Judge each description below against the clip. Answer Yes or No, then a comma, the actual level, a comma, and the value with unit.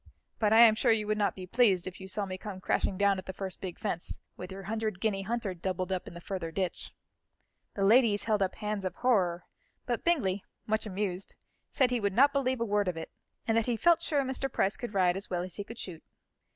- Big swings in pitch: No, average, 3.5 semitones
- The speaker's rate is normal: No, fast, 245 wpm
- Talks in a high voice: Yes, high, 200 Hz